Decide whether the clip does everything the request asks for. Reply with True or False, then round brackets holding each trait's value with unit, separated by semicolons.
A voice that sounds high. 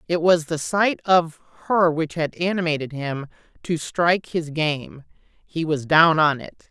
False (160 Hz)